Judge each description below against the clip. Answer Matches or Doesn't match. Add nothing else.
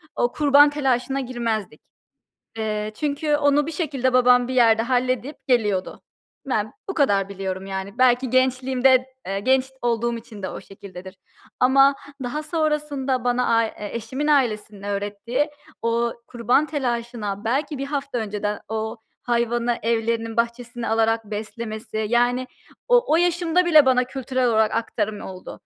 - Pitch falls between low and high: Doesn't match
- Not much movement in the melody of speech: Doesn't match